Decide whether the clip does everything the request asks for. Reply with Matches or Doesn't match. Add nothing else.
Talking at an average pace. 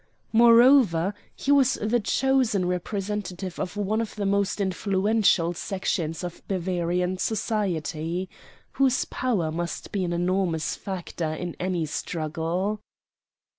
Doesn't match